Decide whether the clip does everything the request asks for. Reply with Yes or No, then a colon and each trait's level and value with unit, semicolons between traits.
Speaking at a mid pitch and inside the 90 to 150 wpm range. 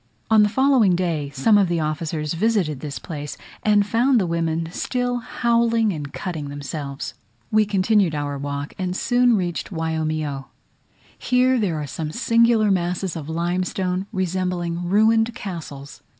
Yes: medium, 180 Hz; average, 145 wpm